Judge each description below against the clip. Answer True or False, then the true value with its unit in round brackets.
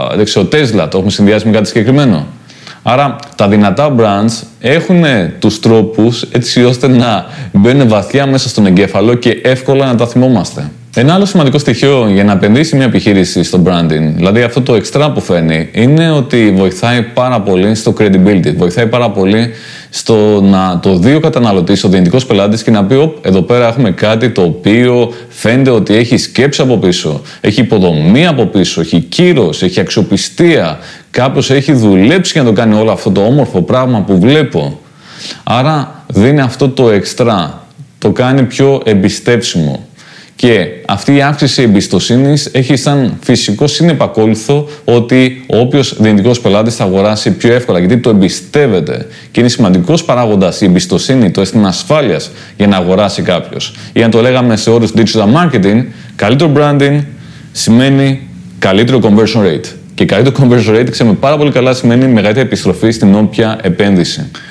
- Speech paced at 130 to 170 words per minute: True (160 wpm)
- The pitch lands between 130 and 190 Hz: False (120 Hz)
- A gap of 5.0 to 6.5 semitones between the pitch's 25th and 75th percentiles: False (4.6 semitones)